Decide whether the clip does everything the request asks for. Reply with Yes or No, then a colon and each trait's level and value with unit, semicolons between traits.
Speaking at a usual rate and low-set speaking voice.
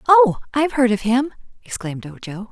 No: average, 165 wpm; high, 245 Hz